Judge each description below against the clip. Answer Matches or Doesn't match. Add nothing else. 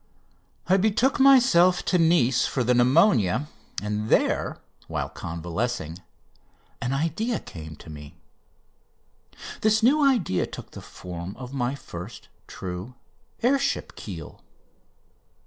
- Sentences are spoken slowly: Matches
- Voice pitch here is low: Matches